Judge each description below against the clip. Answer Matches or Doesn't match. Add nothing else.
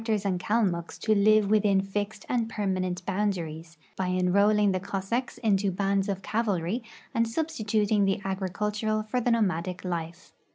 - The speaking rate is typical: Matches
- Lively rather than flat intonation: Doesn't match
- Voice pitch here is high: Matches